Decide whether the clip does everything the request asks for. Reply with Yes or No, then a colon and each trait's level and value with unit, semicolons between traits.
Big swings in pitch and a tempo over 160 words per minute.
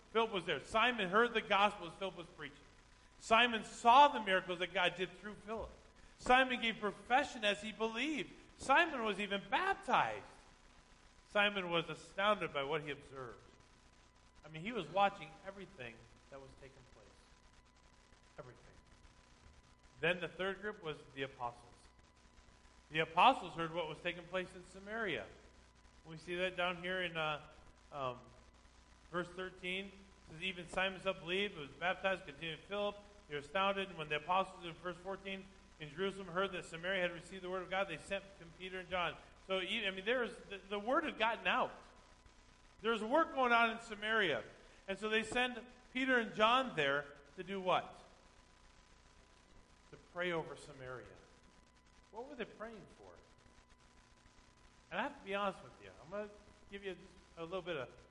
No: average, 4.6 semitones; average, 170 wpm